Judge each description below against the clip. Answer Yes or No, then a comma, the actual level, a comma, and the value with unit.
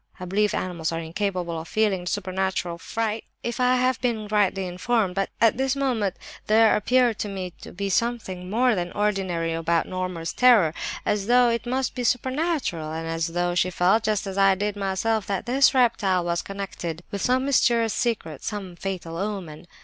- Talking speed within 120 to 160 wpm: No, average, 175 wpm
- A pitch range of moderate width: Yes, average, 4.5 semitones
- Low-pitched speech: No, high, 200 Hz